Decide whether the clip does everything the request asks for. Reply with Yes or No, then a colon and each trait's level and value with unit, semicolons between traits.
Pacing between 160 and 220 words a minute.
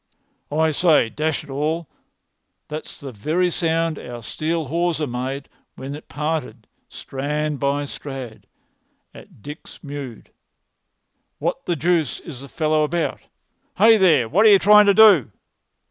No: average, 140 wpm